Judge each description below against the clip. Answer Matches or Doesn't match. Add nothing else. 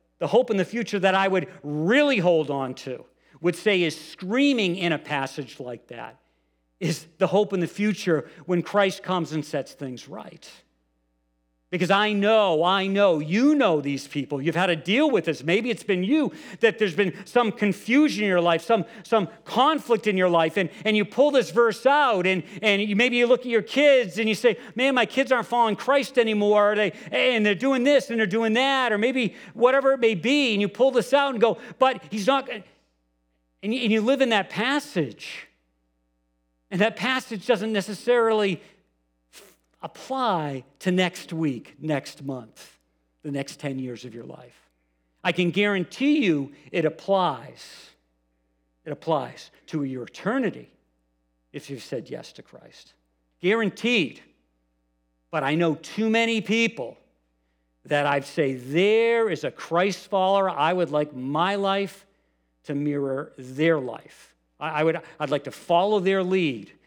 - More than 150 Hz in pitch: Matches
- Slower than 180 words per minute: Matches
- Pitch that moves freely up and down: Matches